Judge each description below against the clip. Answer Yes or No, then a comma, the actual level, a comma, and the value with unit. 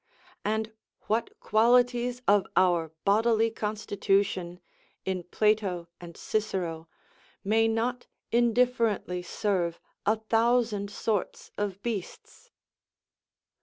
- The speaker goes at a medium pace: No, slow, 90 wpm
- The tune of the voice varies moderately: Yes, average, 3.3 semitones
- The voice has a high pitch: Yes, high, 215 Hz